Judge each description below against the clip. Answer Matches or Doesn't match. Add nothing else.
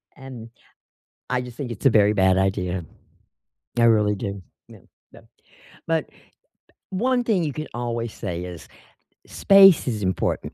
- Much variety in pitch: Matches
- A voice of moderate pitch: Doesn't match